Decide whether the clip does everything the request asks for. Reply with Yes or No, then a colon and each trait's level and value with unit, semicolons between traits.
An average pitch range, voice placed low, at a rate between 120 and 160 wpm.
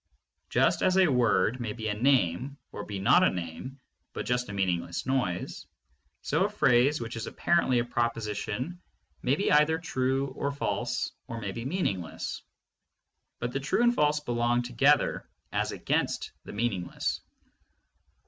Yes: average, 4.9 semitones; low, 120 Hz; average, 155 wpm